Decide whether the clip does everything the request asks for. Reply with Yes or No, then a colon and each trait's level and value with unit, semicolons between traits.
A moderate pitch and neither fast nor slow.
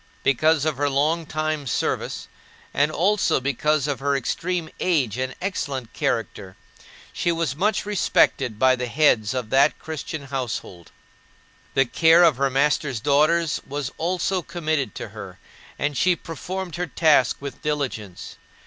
Yes: medium, 145 Hz; average, 145 wpm